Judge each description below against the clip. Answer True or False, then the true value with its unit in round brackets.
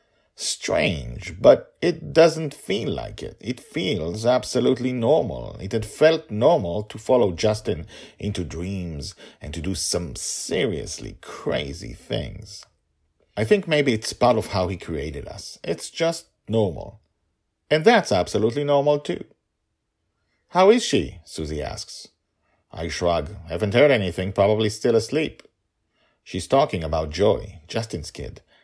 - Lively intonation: True (8.6 semitones)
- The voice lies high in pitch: False (110 Hz)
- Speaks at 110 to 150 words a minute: True (135 wpm)